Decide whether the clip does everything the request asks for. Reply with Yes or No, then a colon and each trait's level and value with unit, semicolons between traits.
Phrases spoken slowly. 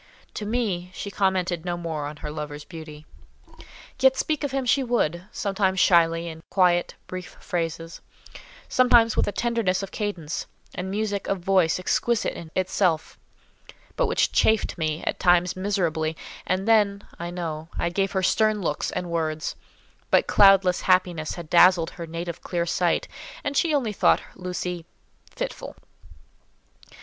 No: average, 150 wpm